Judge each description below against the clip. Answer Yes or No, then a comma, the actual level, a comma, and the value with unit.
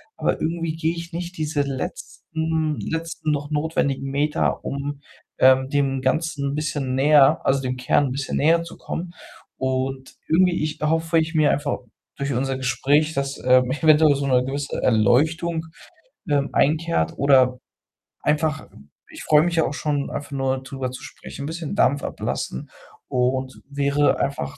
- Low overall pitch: No, medium, 145 Hz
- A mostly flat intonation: No, average, 3.0 semitones